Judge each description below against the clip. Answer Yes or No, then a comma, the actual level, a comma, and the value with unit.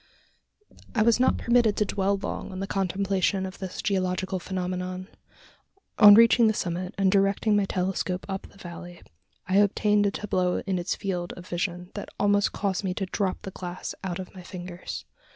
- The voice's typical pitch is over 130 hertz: Yes, high, 190 Hz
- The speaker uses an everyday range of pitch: No, narrow, 1.9 semitones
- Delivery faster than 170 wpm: Yes, average, 180 wpm